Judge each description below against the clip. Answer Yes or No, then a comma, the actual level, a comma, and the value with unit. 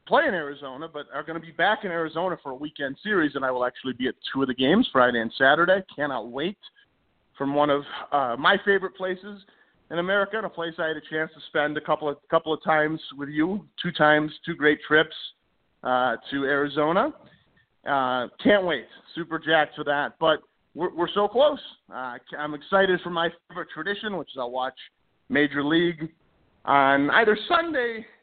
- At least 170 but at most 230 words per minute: Yes, average, 195 wpm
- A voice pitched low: No, medium, 160 Hz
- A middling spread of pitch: Yes, average, 4.3 semitones